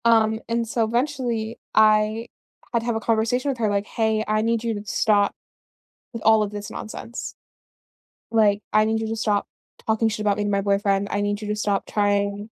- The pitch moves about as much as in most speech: No, narrow, 1.7 semitones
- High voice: Yes, high, 215 Hz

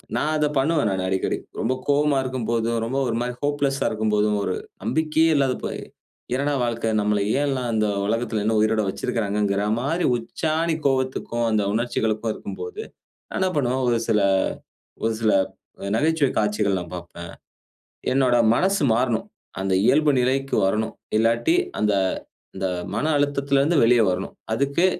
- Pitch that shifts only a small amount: No, average, 4.7 semitones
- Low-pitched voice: Yes, low, 120 Hz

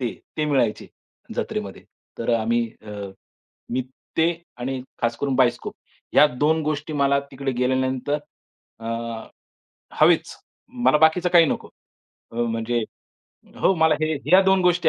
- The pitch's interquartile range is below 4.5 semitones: No, average, 5.1 semitones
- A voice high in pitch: No, low, 135 Hz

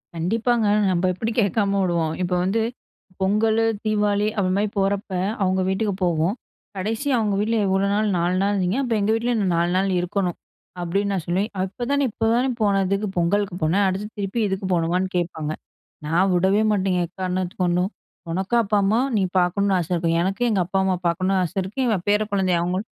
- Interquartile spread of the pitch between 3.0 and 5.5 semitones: No, narrow, 2.6 semitones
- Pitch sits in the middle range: No, high, 195 Hz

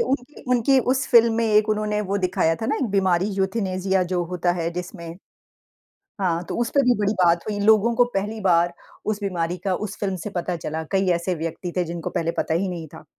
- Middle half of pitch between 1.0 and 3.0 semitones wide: No, average, 3.5 semitones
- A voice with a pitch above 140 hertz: Yes, high, 190 Hz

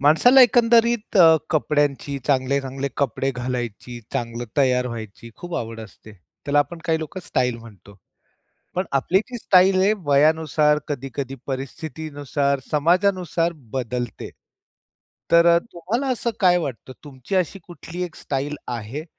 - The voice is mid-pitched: Yes, medium, 145 Hz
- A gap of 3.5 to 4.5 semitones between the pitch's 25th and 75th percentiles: No, average, 5.2 semitones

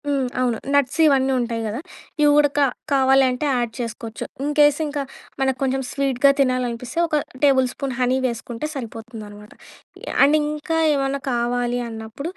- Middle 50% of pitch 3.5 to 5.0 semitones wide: No, average, 2.7 semitones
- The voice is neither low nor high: No, very high, 260 Hz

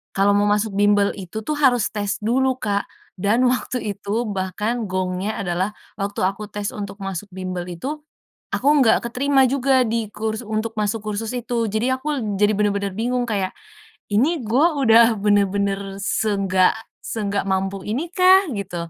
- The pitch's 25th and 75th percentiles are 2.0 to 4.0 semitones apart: Yes, average, 2.8 semitones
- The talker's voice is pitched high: Yes, high, 205 Hz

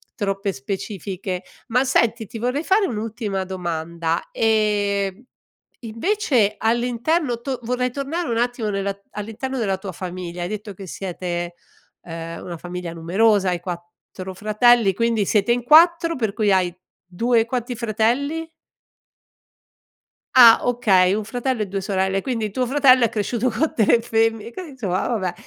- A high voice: Yes, high, 215 Hz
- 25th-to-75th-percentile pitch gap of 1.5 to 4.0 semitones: No, average, 4.4 semitones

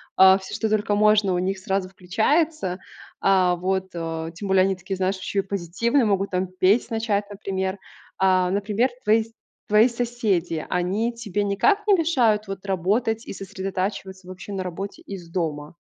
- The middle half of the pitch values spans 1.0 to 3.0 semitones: Yes, narrow, 2.6 semitones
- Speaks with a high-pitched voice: Yes, high, 195 Hz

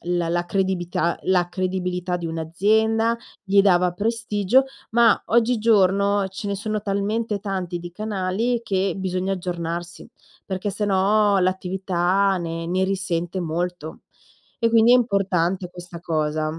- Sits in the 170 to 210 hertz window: Yes, high, 190 Hz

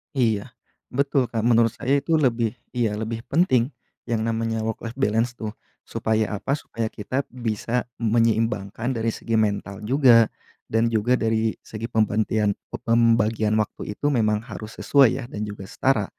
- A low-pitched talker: Yes, low, 115 Hz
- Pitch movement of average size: No, narrow, 2.1 semitones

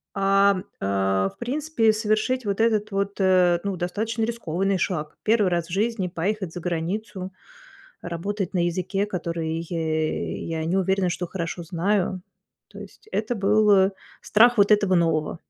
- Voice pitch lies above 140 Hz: Yes, high, 190 Hz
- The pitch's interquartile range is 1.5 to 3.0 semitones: No, average, 3.7 semitones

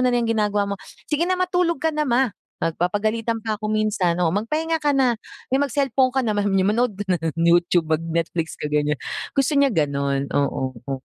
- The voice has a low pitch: No, high, 215 Hz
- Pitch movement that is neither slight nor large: No, wide, 8.0 semitones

